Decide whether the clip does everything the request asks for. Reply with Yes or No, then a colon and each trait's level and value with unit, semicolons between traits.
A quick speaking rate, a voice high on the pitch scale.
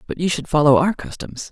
No: fast, 240 wpm; medium, 150 Hz